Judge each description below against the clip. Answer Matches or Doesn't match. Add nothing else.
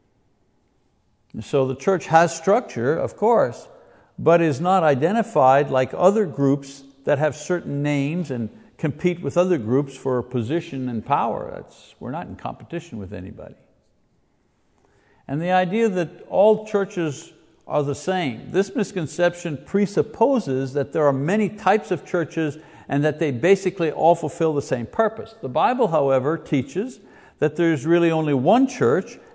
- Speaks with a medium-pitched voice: Matches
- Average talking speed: Matches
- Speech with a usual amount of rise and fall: Matches